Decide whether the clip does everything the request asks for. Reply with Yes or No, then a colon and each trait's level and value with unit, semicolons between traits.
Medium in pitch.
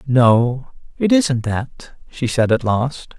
No: low, 130 Hz